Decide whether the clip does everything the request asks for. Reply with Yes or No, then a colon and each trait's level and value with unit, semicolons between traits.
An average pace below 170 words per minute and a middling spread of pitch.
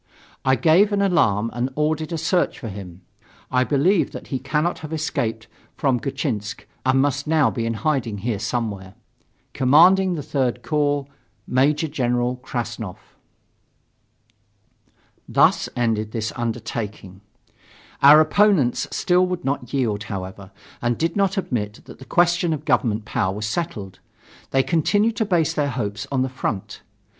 No: average, 145 wpm; wide, 5.9 semitones